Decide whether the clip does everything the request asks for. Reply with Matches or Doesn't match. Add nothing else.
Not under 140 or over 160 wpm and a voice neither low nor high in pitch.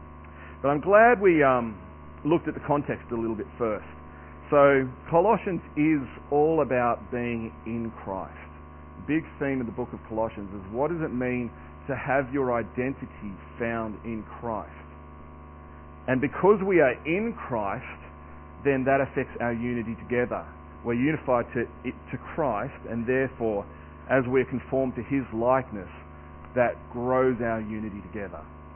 Doesn't match